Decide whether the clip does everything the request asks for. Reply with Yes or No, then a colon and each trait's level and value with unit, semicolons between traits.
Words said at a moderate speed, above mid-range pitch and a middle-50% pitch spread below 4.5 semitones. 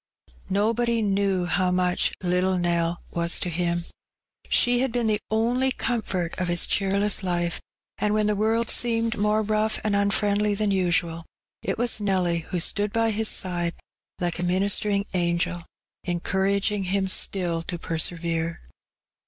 Yes: average, 150 wpm; high, 195 Hz; average, 3.4 semitones